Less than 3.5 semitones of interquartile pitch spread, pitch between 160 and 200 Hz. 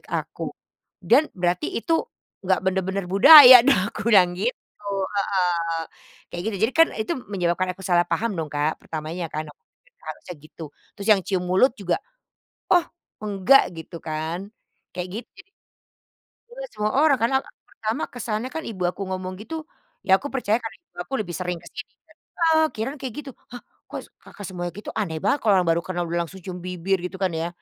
No: average, 4.9 semitones; high, 190 Hz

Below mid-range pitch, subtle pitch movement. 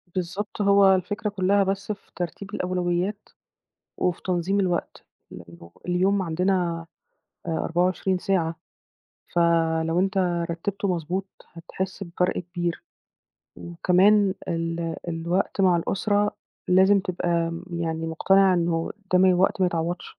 No: medium, 180 Hz; narrow, 2.3 semitones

